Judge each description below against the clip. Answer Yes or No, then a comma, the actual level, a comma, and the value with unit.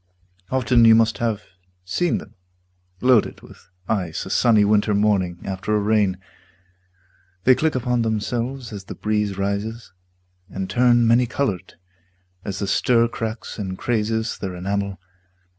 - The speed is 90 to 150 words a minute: Yes, average, 140 wpm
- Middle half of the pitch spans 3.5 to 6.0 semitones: No, average, 3.0 semitones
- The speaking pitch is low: Yes, low, 110 Hz